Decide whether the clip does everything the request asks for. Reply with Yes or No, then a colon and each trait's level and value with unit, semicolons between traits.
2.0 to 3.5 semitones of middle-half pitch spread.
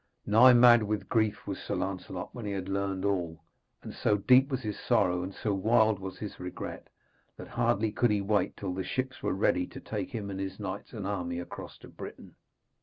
Yes: average, 2.7 semitones